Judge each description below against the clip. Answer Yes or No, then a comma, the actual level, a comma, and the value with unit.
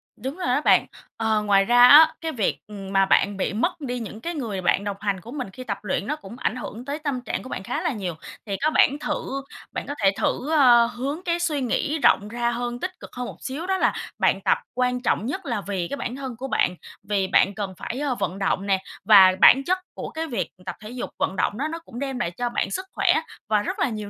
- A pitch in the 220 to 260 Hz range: Yes, high, 245 Hz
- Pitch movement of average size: No, wide, 5.9 semitones